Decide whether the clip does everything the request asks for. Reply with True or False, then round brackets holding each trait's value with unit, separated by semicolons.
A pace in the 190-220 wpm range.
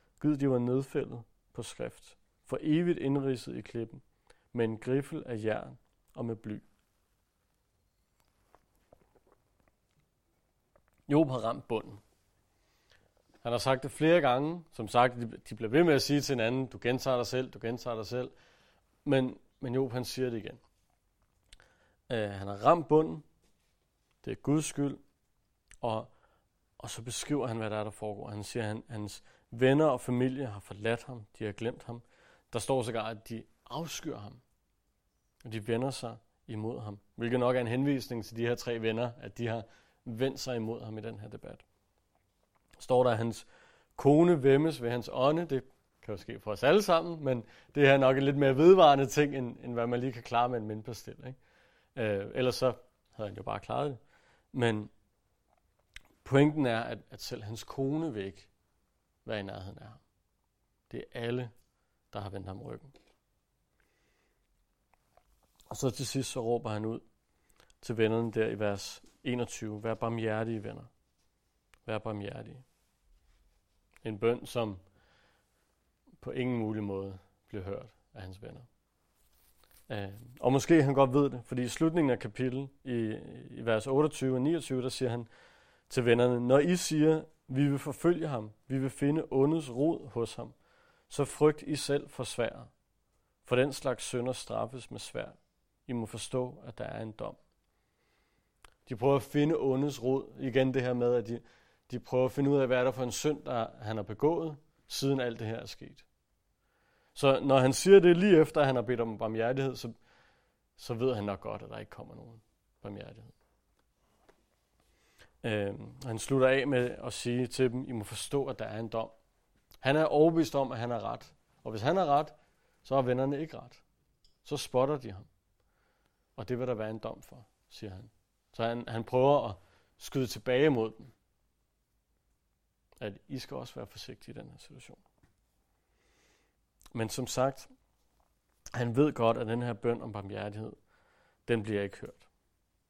False (175 wpm)